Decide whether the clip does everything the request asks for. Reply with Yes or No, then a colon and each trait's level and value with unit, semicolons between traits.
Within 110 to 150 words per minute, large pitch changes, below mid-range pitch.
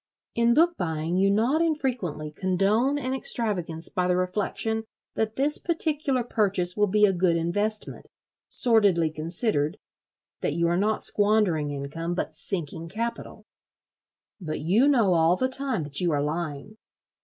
No: average, 145 wpm; wide, 5.9 semitones; high, 195 Hz